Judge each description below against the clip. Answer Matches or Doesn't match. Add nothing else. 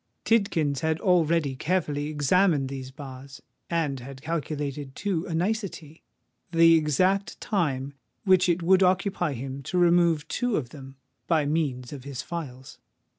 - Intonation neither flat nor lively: Matches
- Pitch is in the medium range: Matches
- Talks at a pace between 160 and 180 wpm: Doesn't match